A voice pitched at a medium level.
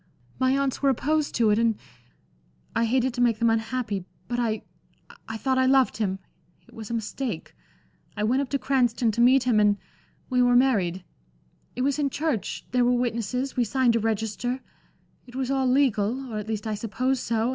No: high, 245 Hz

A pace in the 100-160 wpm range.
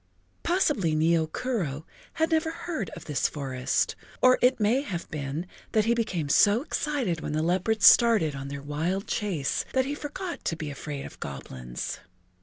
No: average, 170 wpm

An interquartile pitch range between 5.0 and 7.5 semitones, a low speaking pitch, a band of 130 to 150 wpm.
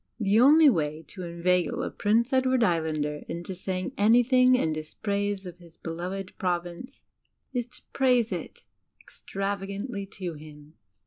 No: average, 5.3 semitones; high, 195 Hz; slow, 135 wpm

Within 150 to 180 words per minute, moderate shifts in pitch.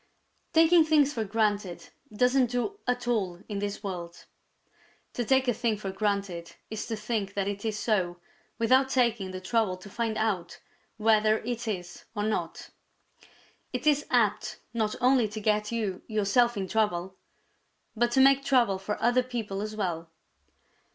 Yes: average, 165 wpm; average, 3.5 semitones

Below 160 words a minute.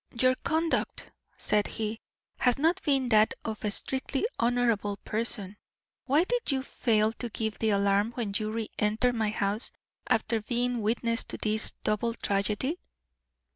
Yes: average, 150 wpm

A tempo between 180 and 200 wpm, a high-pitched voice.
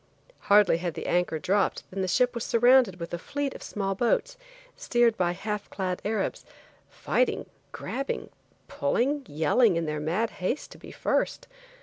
No: average, 160 wpm; high, 205 Hz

